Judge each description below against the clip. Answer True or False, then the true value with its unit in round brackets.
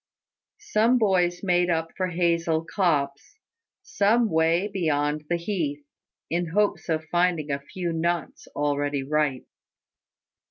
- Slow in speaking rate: True (120 wpm)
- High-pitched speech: False (170 Hz)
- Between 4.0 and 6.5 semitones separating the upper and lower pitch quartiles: False (3.4 semitones)